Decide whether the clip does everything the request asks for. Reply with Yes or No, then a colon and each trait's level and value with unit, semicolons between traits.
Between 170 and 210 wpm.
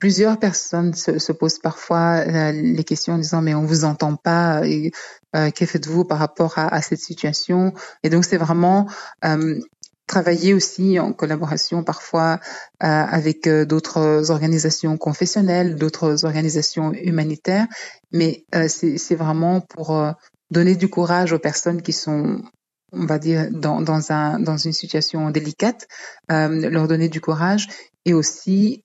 No: average, 155 wpm